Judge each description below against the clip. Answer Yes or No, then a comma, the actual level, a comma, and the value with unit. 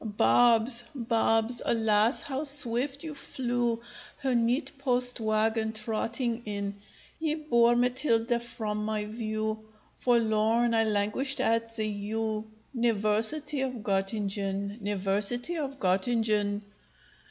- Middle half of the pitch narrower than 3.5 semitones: Yes, narrow, 2.4 semitones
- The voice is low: No, high, 225 Hz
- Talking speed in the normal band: No, slow, 110 wpm